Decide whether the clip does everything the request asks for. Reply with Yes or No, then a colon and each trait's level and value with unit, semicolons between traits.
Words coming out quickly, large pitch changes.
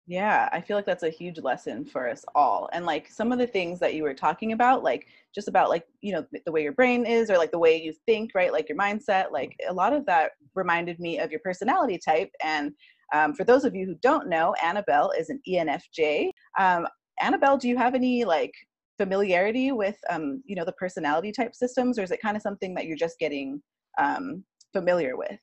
Yes: fast, 225 wpm; wide, 6.7 semitones